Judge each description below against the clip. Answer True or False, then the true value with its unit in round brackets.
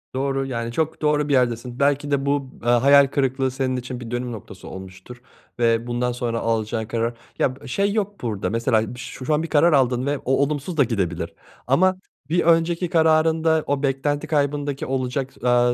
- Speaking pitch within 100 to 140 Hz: True (135 Hz)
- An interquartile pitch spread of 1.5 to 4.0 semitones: True (3.4 semitones)